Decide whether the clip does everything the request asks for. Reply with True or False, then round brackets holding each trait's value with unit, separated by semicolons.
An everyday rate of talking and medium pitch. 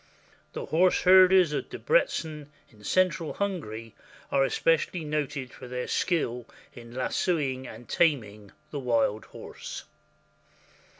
False (115 wpm; 145 Hz)